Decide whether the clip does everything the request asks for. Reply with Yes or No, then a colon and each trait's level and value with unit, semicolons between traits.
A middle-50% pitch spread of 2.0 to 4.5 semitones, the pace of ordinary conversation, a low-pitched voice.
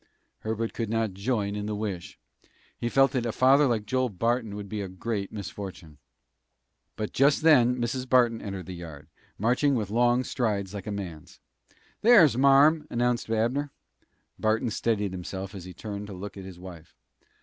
Yes: average, 3.9 semitones; average, 170 wpm; low, 110 Hz